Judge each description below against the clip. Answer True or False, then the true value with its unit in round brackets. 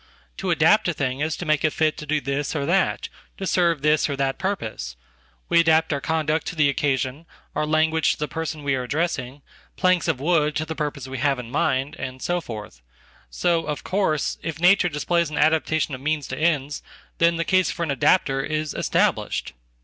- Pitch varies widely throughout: False (2.9 semitones)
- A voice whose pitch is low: False (150 Hz)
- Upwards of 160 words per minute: True (190 wpm)